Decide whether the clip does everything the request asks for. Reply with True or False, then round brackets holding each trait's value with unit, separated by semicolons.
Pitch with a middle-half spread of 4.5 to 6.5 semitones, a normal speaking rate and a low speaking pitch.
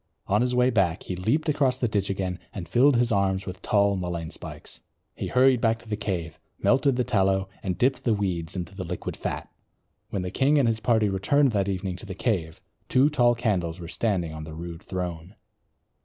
False (5.1 semitones; 210 wpm; 100 Hz)